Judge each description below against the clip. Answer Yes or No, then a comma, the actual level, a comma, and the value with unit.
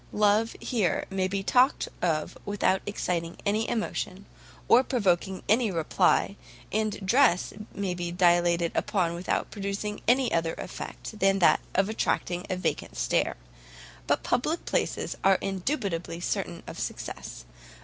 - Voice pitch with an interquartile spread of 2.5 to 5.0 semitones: Yes, average, 3.6 semitones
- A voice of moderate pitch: No, high, 195 Hz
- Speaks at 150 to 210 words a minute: No, slow, 135 wpm